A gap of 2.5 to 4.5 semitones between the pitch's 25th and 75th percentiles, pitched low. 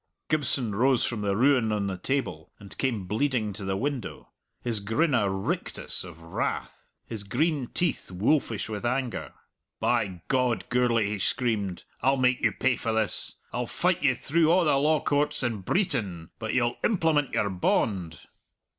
No: average, 5.3 semitones; low, 115 Hz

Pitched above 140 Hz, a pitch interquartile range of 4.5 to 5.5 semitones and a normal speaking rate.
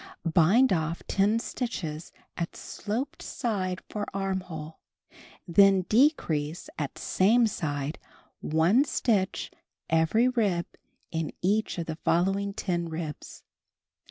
No: medium, 185 Hz; average, 4.8 semitones; slow, 105 wpm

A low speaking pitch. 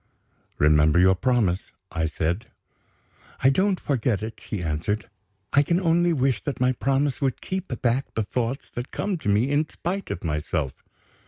Yes: low, 125 Hz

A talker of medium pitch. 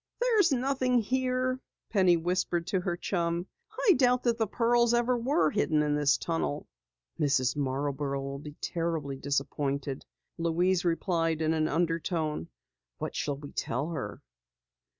Yes: medium, 170 Hz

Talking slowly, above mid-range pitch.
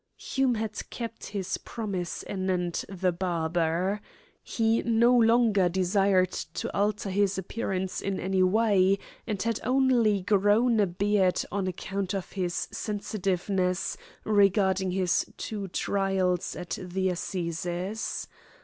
Yes: slow, 120 wpm; high, 195 Hz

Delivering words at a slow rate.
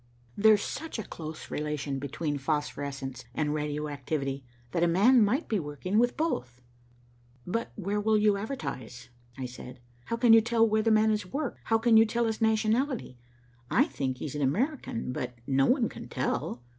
No: average, 180 wpm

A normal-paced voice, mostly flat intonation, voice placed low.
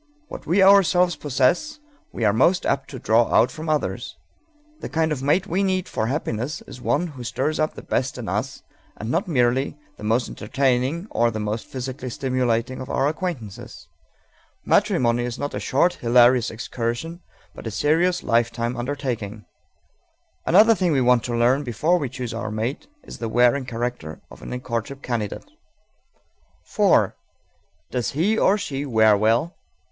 No: average, 165 wpm; average, 4.8 semitones; low, 130 Hz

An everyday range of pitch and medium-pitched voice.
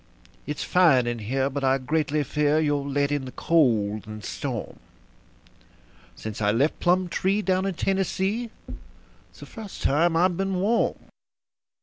No: wide, 5.7 semitones; medium, 150 Hz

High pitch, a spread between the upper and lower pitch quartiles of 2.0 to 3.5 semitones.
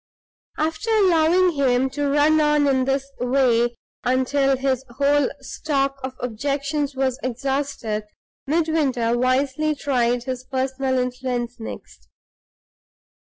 Yes: very high, 270 Hz; narrow, 2.4 semitones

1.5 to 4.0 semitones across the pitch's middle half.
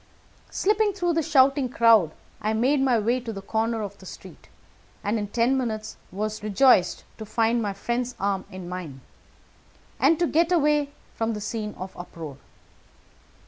No: average, 4.8 semitones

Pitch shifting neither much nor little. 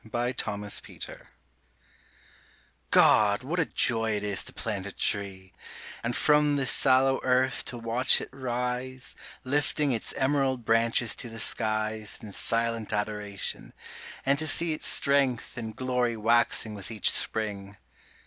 Yes: average, 3.3 semitones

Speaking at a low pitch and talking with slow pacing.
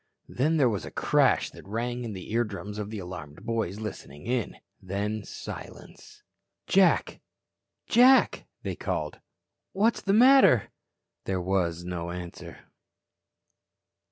Yes: low, 105 Hz; slow, 125 wpm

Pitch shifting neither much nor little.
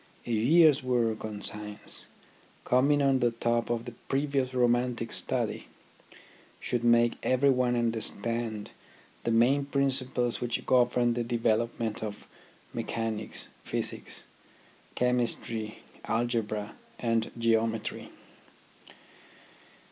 No: narrow, 1.9 semitones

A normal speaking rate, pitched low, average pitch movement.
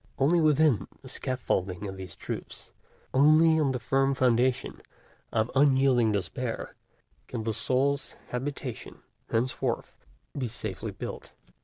No: slow, 120 wpm; low, 130 Hz; average, 3.5 semitones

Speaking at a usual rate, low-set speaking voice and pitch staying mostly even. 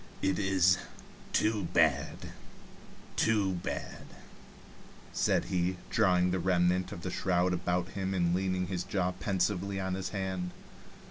No: slow, 130 wpm; very low, 95 Hz; narrow, 1.2 semitones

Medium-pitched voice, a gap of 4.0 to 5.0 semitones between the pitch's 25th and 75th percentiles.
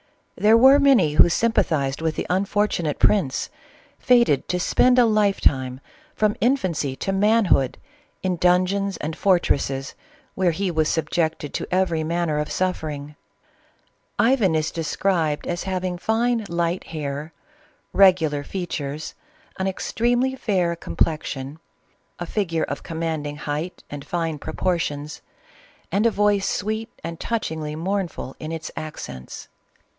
Yes: medium, 175 Hz; average, 4.6 semitones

